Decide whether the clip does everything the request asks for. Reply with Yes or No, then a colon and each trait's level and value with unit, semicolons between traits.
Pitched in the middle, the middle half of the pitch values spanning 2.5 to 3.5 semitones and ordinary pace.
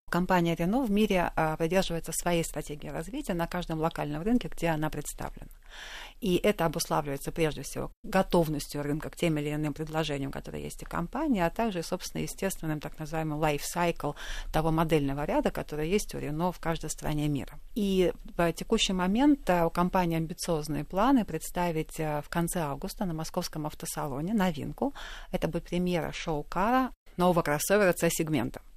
Yes: medium, 165 Hz; average, 3.1 semitones; average, 150 wpm